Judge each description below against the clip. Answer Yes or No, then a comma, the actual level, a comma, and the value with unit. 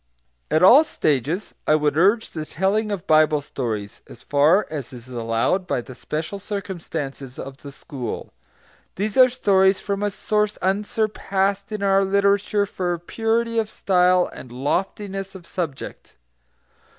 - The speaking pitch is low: No, high, 190 Hz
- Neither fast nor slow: Yes, average, 145 wpm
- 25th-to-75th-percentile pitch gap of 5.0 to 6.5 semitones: Yes, wide, 5.5 semitones